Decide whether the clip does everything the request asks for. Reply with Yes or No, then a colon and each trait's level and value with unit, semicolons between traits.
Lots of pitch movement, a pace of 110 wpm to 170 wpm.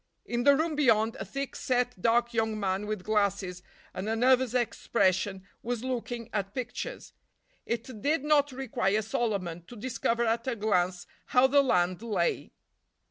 No: average, 3.9 semitones; average, 160 wpm